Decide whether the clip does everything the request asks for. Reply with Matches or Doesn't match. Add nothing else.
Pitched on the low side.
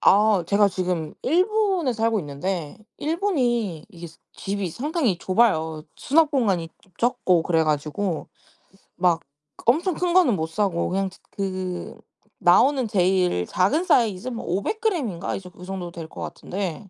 Doesn't match